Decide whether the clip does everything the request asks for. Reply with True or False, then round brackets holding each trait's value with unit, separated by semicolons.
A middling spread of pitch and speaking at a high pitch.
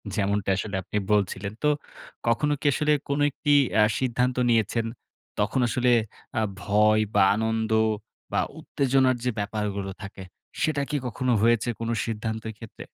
False (3.4 semitones; 110 Hz)